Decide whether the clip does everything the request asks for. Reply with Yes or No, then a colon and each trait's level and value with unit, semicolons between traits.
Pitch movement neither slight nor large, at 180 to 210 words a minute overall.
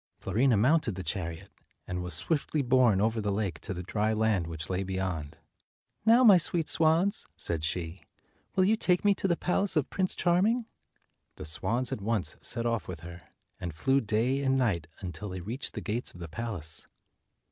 No: wide, 7.8 semitones; average, 190 wpm